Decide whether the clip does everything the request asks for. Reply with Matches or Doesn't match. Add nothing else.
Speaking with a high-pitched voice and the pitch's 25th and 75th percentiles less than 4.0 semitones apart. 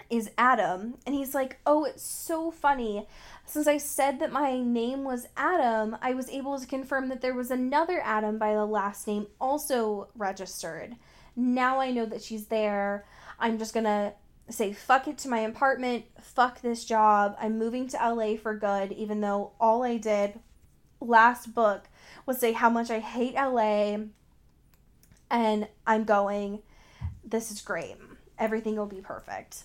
Matches